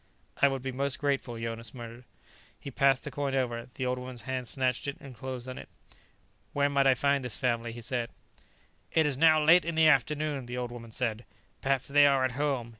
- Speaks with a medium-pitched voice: No, low, 130 Hz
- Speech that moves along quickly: Yes, fast, 215 wpm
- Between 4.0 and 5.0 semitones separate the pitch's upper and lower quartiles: No, narrow, 2.5 semitones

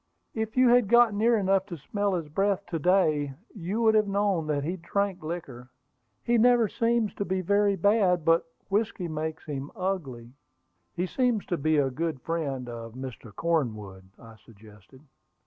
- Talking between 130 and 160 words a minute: No, average, 170 wpm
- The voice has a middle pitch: Yes, medium, 175 Hz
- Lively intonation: Yes, wide, 6.5 semitones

